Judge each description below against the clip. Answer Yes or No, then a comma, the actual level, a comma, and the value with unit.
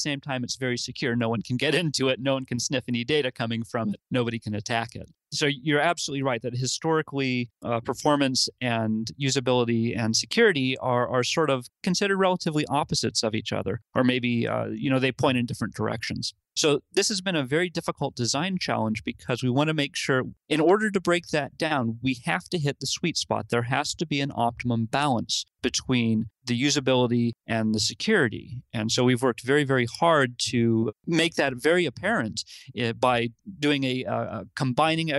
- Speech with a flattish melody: No, average, 3.9 semitones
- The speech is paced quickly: No, average, 195 wpm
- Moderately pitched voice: No, low, 130 Hz